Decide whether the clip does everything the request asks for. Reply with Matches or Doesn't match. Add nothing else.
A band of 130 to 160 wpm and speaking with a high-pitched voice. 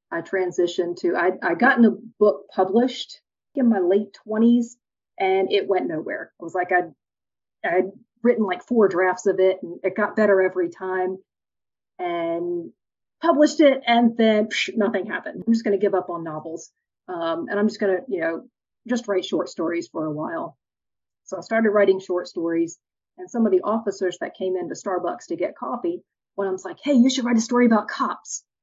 Doesn't match